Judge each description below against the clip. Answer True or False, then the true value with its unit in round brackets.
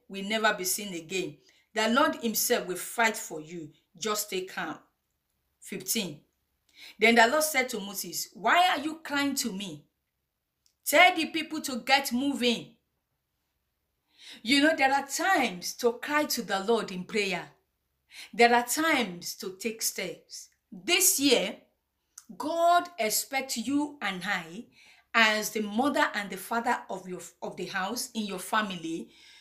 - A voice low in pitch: False (220 Hz)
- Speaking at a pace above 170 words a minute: False (150 wpm)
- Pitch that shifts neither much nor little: False (6.7 semitones)